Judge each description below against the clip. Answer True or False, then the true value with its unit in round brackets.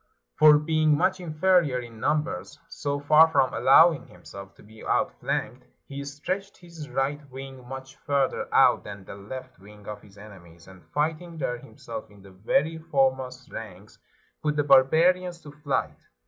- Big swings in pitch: True (6.0 semitones)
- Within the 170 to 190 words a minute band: False (160 wpm)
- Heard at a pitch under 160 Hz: True (140 Hz)